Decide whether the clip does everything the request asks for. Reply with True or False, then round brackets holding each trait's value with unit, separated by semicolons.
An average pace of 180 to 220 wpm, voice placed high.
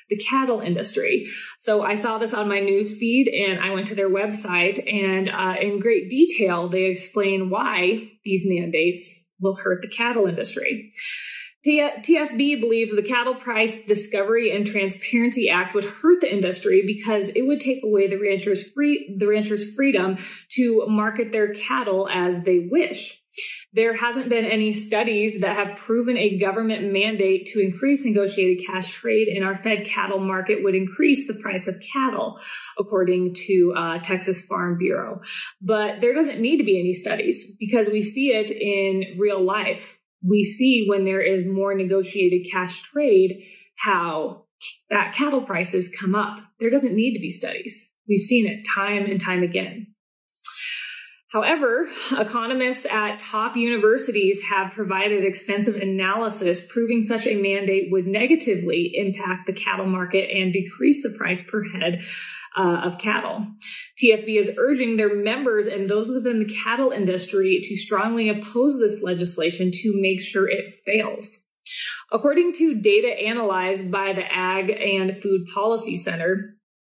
False (155 wpm; 205 Hz)